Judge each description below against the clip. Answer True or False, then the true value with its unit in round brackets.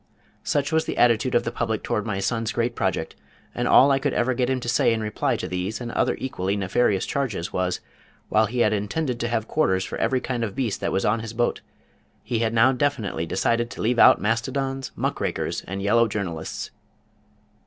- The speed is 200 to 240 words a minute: True (205 wpm)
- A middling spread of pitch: True (3.6 semitones)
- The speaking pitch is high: False (115 Hz)